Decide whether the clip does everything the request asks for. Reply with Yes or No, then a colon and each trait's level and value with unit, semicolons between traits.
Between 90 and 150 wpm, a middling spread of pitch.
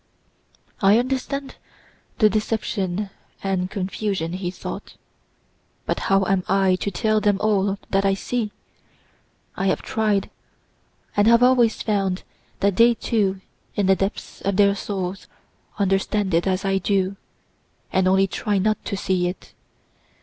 No: average, 140 wpm; narrow, 2.0 semitones